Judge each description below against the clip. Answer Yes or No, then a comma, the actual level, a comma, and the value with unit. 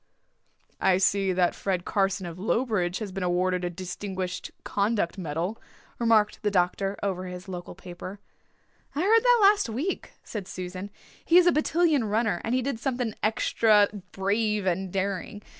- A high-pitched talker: Yes, high, 200 Hz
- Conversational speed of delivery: Yes, average, 160 wpm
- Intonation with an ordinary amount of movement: Yes, average, 3.7 semitones